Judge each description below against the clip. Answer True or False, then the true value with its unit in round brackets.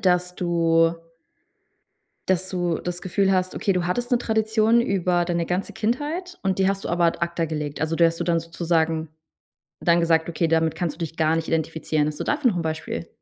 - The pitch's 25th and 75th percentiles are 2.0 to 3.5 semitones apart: True (2.7 semitones)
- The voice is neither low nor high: True (175 Hz)